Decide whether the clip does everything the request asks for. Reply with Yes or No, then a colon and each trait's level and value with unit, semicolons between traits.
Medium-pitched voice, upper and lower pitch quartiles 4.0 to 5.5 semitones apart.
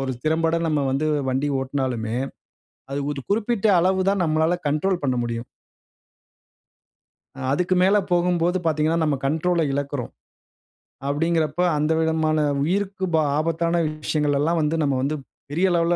No: medium, 160 Hz; average, 3.2 semitones